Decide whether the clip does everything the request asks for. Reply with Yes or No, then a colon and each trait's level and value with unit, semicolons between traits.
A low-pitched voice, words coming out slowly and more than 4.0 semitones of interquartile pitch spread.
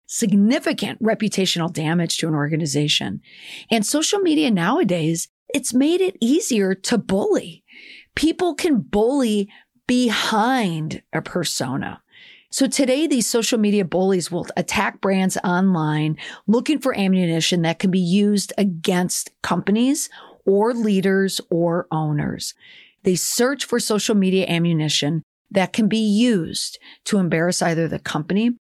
No: high, 200 Hz; slow, 125 wpm; wide, 5.6 semitones